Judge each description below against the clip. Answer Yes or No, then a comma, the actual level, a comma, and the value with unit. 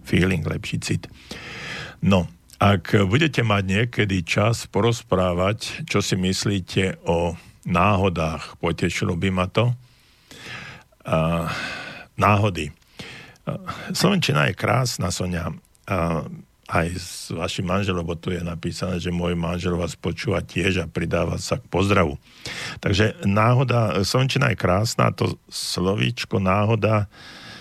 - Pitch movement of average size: Yes, average, 3.7 semitones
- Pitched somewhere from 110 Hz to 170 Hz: No, very low, 95 Hz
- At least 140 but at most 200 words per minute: No, average, 115 wpm